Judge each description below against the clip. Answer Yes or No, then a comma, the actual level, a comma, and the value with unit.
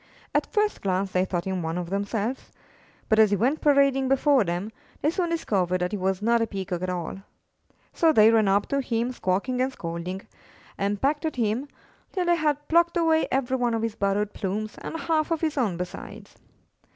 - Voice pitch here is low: No, high, 225 Hz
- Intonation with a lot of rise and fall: Yes, wide, 6.8 semitones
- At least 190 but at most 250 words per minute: Yes, average, 200 wpm